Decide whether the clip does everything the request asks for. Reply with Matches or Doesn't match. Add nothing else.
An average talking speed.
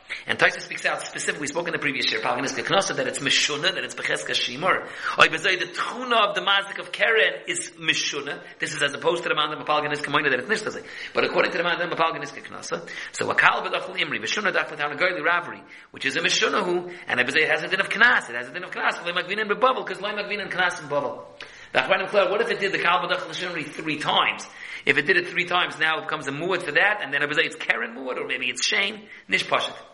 Doesn't match